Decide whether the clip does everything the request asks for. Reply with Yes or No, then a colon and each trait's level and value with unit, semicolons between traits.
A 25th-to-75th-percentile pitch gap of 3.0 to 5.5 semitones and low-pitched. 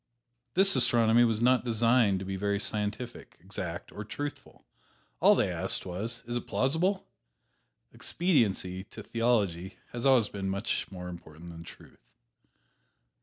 Yes: average, 4.1 semitones; low, 110 Hz